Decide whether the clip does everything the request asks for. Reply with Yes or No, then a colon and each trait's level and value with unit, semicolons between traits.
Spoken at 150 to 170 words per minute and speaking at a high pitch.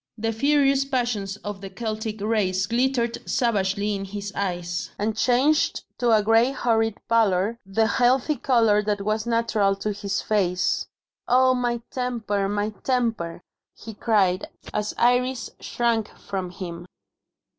No: slow, 135 wpm; high, 220 Hz